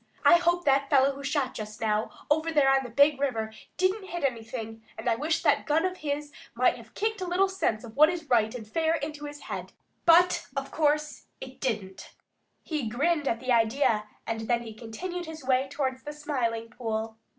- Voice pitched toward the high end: Yes, very high, 275 Hz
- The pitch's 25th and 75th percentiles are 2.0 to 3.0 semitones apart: No, wide, 5.6 semitones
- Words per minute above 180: Yes, fast, 205 wpm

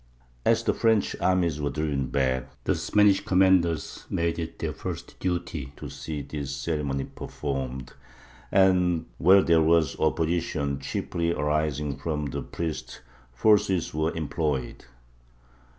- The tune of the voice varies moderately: Yes, average, 3.5 semitones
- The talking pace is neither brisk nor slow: No, slow, 125 wpm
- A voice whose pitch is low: Yes, very low, 80 Hz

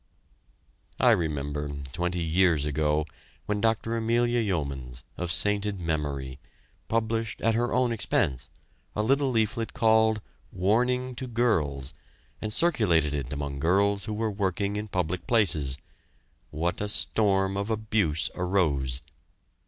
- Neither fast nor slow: No, slow, 125 wpm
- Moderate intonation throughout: No, wide, 6.6 semitones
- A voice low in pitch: Yes, low, 100 Hz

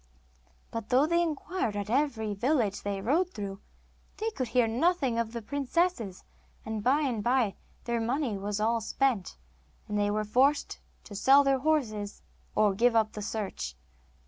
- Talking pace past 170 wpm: No, average, 165 wpm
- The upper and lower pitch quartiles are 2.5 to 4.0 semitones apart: No, average, 4.8 semitones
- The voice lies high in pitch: Yes, high, 235 Hz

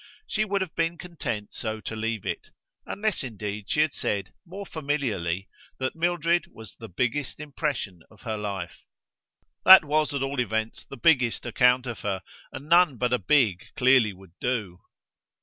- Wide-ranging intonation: Yes, wide, 6.3 semitones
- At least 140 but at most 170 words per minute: Yes, average, 165 wpm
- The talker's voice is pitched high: No, low, 125 Hz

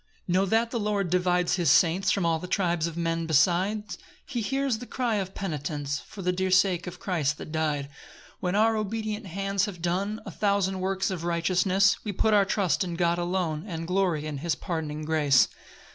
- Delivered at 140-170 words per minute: No, fast, 205 wpm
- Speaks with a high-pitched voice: No, medium, 180 Hz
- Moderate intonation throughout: Yes, average, 3.2 semitones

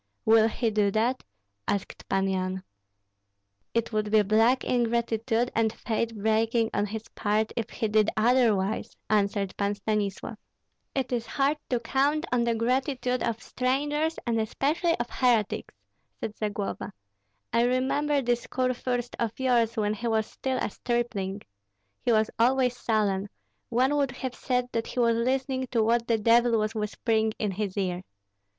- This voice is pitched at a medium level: No, high, 230 Hz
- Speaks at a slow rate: No, average, 155 wpm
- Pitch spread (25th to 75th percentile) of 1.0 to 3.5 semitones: Yes, average, 2.7 semitones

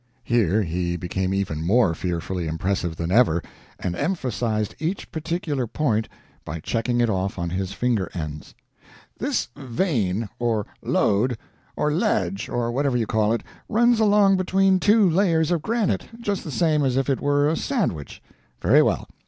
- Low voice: Yes, low, 120 Hz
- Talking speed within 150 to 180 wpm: Yes, average, 160 wpm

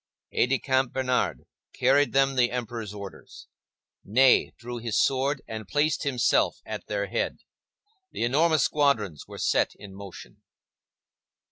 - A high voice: No, low, 125 Hz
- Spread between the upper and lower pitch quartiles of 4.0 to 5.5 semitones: Yes, average, 4.4 semitones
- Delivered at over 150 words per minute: No, slow, 135 wpm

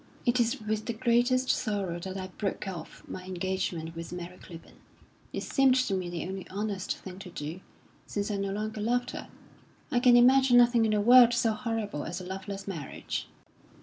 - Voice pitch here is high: Yes, high, 205 Hz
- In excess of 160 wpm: Yes, average, 190 wpm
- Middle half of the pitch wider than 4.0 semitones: Yes, average, 4.4 semitones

